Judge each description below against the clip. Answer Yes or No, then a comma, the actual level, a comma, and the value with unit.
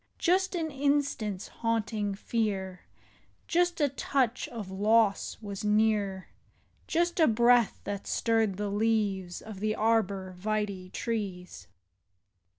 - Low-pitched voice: No, high, 215 Hz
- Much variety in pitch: No, average, 3.2 semitones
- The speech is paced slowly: Yes, slow, 115 wpm